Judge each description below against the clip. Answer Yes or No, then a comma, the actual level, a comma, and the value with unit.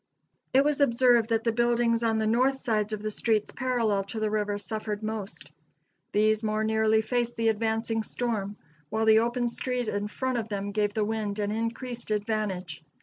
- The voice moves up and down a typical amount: No, narrow, 1.9 semitones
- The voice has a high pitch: Yes, high, 220 Hz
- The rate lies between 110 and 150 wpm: No, average, 185 wpm